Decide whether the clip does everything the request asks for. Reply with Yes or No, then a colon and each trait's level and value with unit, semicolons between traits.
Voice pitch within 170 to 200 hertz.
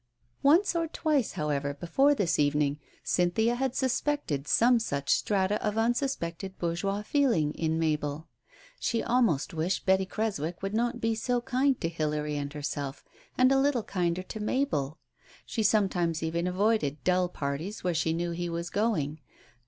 Yes: medium, 185 Hz